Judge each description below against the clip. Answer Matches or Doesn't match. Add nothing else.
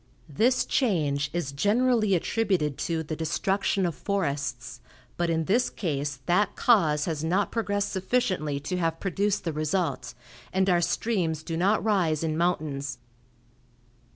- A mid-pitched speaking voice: Matches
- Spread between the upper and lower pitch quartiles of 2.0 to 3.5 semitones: Doesn't match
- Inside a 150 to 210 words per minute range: Doesn't match